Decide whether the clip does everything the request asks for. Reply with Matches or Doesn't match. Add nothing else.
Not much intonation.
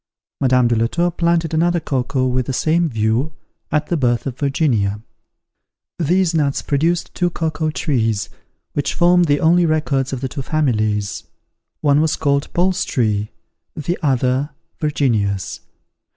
Doesn't match